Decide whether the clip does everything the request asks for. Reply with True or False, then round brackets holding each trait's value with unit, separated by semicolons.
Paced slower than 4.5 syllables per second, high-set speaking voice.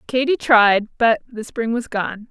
True (3.8 syllables/s; 230 Hz)